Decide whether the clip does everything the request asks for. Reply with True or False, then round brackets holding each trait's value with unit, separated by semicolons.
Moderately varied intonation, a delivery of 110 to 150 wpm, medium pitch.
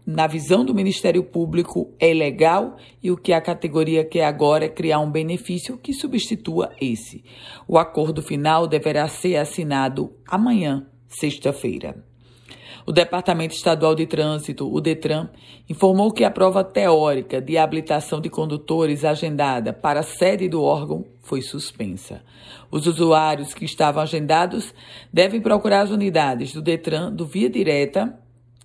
True (3.0 semitones; 140 wpm; 160 Hz)